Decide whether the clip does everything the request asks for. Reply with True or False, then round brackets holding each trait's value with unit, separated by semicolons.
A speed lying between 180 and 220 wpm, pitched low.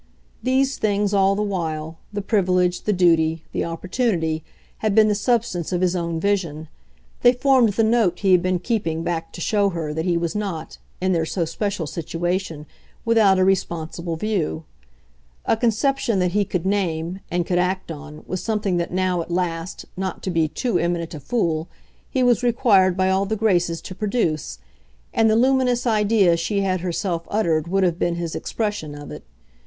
False (185 wpm; 185 Hz)